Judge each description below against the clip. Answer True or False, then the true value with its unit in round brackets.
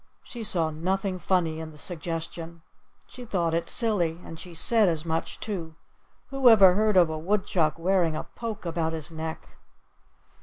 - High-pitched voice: False (170 Hz)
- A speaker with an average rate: True (165 wpm)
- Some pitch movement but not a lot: True (3.3 semitones)